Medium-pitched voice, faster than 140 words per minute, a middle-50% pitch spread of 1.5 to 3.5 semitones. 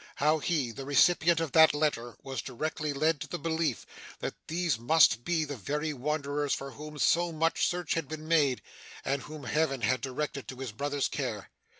Yes: medium, 150 Hz; average, 190 wpm; average, 2.9 semitones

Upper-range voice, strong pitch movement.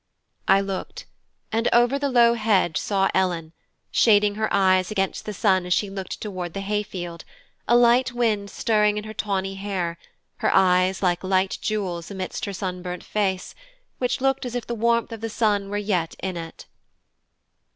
No: high, 200 Hz; average, 2.9 semitones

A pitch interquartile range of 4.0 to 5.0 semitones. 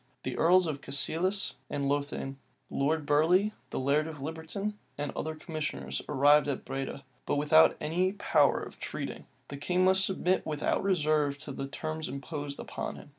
No: average, 3.1 semitones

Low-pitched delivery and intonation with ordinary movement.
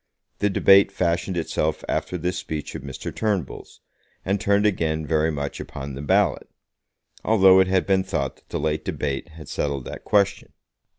Yes: very low, 85 Hz; average, 4.2 semitones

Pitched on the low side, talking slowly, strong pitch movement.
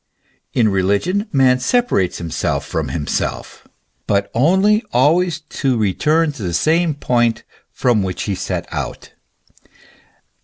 Yes: low, 130 Hz; slow, 120 wpm; wide, 8.6 semitones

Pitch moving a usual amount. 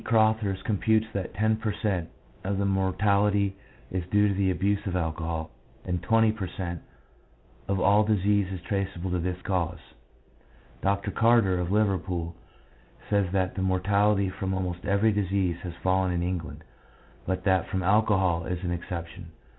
No: narrow, 2.1 semitones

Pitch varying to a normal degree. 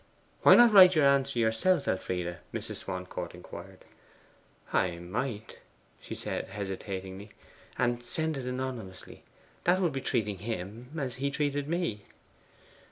No: wide, 6.5 semitones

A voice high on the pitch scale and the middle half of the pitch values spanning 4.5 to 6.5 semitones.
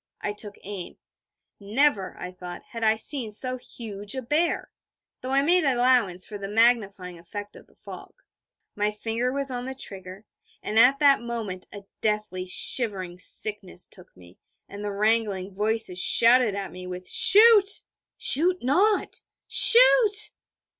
Yes: high, 220 Hz; average, 4.8 semitones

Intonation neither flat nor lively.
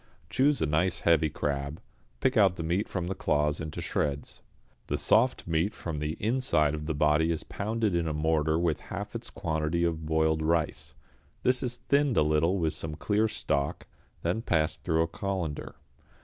Yes: average, 3.8 semitones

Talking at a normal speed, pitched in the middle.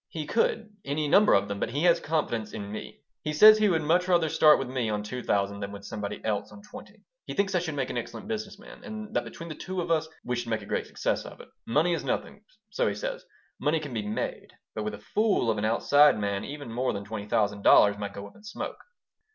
No: fast, 255 wpm; medium, 145 Hz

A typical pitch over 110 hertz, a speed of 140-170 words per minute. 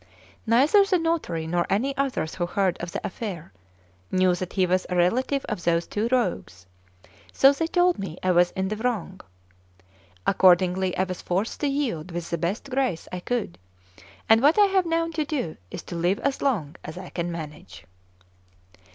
No: high, 190 Hz; average, 185 wpm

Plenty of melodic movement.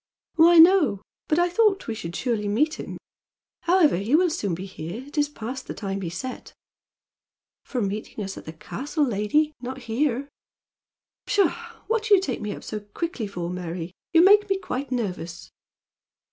Yes: wide, 8.5 semitones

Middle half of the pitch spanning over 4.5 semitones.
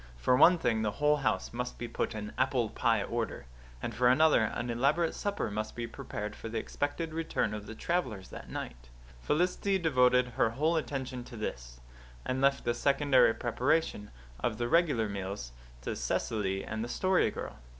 Yes: average, 5.2 semitones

